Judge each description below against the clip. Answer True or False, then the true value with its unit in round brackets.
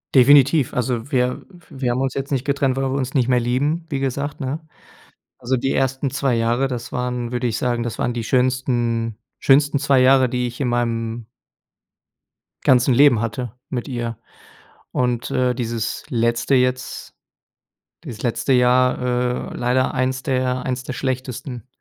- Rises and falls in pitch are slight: True (1.7 semitones)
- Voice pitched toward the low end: True (125 Hz)